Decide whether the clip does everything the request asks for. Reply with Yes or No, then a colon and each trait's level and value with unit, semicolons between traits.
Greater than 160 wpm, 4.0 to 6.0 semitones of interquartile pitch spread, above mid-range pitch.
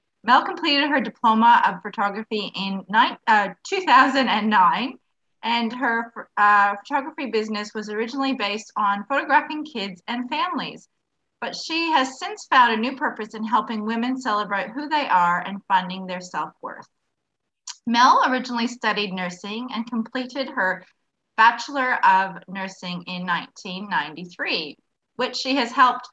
No: slow, 135 wpm; average, 4.6 semitones; high, 225 Hz